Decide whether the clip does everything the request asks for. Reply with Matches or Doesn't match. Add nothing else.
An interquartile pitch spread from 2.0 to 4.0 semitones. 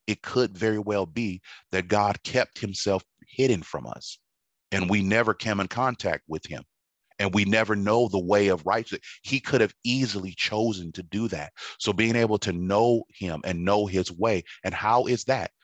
Matches